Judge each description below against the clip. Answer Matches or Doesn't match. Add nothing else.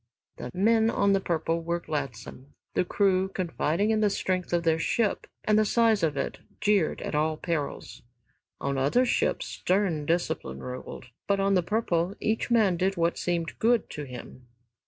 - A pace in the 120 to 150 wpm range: Doesn't match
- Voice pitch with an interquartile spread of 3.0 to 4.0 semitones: Doesn't match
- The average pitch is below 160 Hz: Doesn't match